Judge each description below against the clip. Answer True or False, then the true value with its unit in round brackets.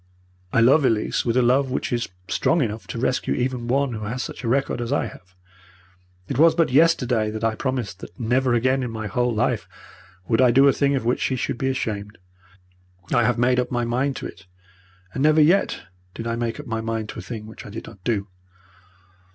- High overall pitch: False (120 Hz)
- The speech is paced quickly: True (225 wpm)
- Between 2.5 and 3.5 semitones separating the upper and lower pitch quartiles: True (2.8 semitones)